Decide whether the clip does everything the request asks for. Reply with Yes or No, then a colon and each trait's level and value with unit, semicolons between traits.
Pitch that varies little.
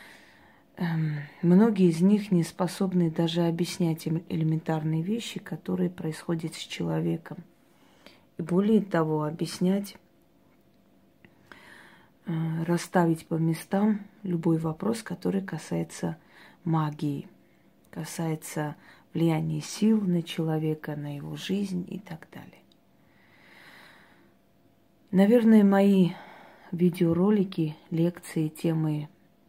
No: average, 3.0 semitones